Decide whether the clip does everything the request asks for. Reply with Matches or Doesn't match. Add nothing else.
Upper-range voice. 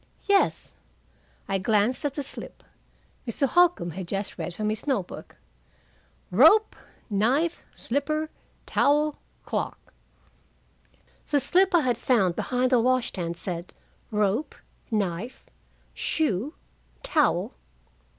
Matches